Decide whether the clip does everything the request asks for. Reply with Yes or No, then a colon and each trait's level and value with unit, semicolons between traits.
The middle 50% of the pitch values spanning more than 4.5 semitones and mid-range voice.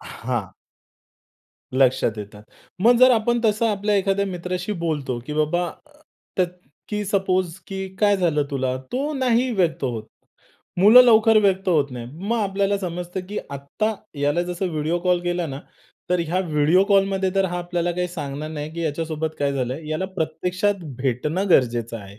Yes: average, 5.1 semitones; medium, 175 Hz